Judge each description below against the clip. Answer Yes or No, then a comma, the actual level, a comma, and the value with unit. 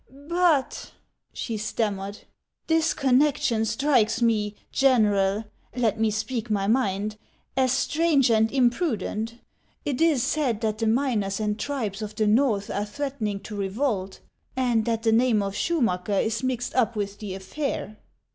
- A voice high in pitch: Yes, high, 225 Hz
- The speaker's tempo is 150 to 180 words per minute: Yes, average, 160 wpm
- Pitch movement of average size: Yes, average, 4.0 semitones